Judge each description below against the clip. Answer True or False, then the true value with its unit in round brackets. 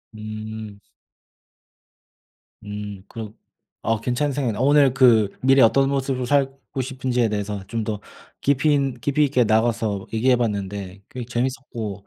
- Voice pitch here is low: True (120 Hz)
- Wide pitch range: False (4.0 semitones)